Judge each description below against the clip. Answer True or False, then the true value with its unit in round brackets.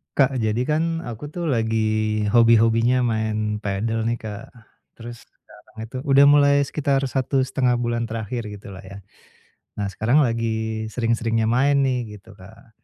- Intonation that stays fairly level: False (3.0 semitones)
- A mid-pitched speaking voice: False (115 Hz)